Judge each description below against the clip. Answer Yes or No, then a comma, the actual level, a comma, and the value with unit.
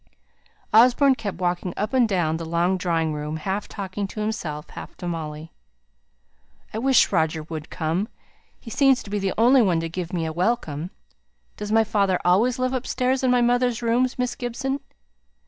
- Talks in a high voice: Yes, high, 200 Hz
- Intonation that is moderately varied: No, wide, 6.5 semitones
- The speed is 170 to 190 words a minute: Yes, average, 180 wpm